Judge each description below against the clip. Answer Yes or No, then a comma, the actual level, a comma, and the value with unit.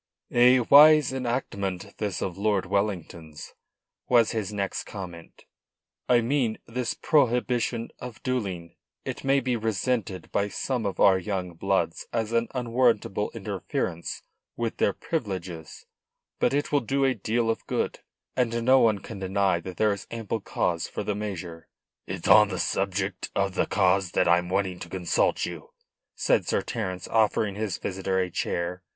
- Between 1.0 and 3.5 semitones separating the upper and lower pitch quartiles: No, average, 4.1 semitones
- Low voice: Yes, low, 105 Hz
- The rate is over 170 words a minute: No, average, 160 wpm